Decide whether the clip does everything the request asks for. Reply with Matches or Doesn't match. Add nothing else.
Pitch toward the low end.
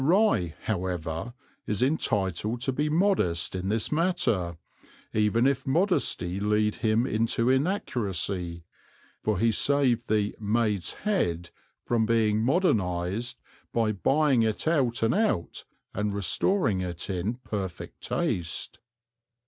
Matches